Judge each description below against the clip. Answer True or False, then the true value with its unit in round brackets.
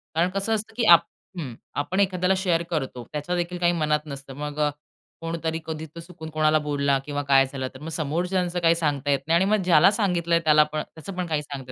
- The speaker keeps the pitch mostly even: False (3.2 semitones)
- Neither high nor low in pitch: True (160 Hz)